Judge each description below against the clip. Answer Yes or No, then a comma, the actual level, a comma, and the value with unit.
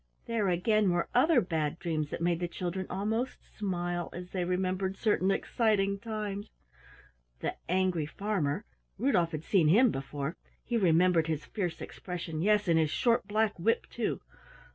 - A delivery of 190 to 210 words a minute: No, average, 155 wpm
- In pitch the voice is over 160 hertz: Yes, medium, 185 Hz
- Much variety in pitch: No, average, 3.8 semitones